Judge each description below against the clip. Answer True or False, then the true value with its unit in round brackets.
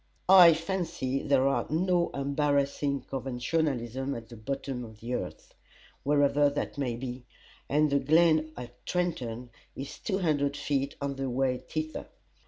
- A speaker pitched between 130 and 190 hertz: True (140 Hz)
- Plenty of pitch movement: False (3.2 semitones)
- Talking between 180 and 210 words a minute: False (145 wpm)